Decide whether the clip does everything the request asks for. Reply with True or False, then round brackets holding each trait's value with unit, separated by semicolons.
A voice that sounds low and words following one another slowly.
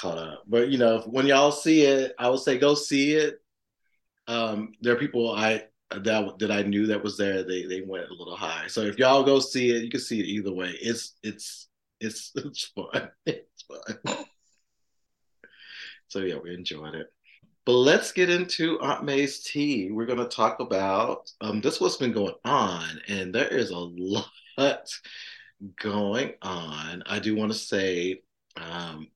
False (110 Hz; 180 wpm)